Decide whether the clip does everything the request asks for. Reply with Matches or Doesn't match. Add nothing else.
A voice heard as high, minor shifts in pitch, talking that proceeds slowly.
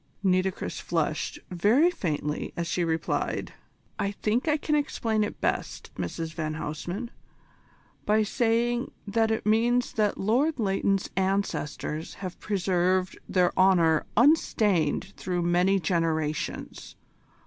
Doesn't match